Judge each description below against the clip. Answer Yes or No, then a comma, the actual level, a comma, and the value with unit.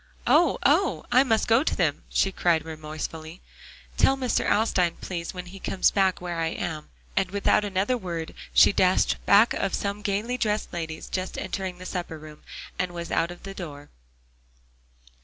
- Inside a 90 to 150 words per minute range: No, average, 175 wpm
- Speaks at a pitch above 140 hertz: Yes, medium, 185 Hz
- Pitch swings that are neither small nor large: Yes, average, 3.8 semitones